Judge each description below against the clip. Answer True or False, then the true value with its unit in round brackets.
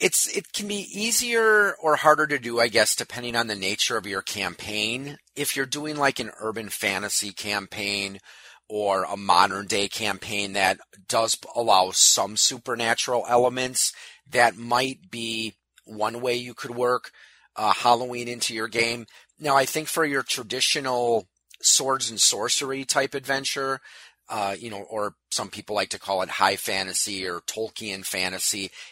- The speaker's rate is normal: True (160 wpm)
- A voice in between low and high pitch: False (120 Hz)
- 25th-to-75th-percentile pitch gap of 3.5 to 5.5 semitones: True (4.6 semitones)